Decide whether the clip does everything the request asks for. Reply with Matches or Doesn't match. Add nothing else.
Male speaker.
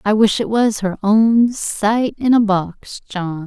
Doesn't match